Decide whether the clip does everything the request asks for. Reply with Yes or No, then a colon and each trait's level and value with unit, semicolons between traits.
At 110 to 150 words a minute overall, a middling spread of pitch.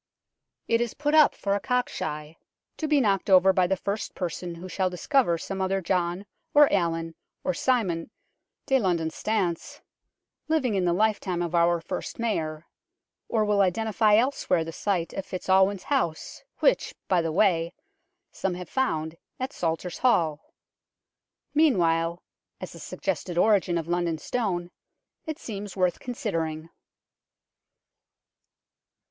Yes: average, 145 wpm; average, 4.4 semitones